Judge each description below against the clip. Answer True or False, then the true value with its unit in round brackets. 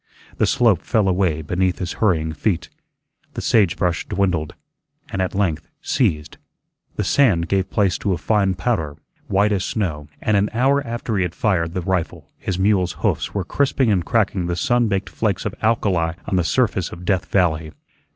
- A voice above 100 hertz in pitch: False (95 Hz)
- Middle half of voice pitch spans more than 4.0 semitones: False (3.6 semitones)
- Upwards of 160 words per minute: True (180 wpm)